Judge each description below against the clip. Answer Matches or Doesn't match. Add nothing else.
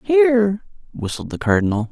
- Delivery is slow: Matches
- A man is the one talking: Matches